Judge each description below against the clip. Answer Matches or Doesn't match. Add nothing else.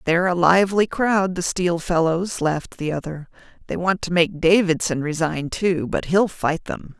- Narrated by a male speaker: Doesn't match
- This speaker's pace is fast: Doesn't match